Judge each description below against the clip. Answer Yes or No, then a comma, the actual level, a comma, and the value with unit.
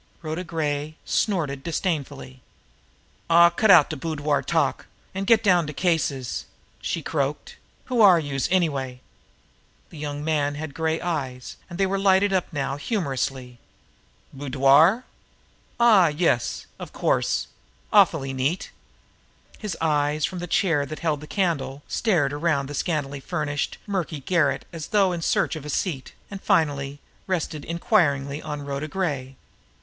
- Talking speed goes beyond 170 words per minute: No, average, 140 wpm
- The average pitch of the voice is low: No, medium, 155 Hz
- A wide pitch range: No, average, 4.0 semitones